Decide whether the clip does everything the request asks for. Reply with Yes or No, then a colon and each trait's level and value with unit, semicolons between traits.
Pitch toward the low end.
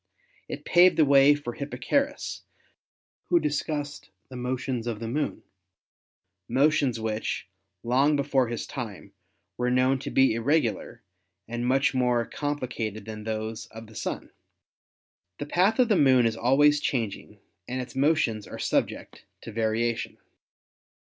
Yes: low, 130 Hz